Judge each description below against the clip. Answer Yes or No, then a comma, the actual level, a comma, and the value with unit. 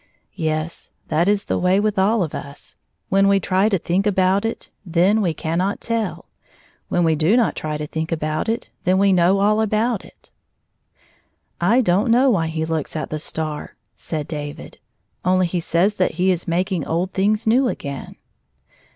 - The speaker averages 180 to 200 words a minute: Yes, average, 190 wpm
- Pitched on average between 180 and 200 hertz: Yes, medium, 185 Hz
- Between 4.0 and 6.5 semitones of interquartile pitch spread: Yes, average, 4.3 semitones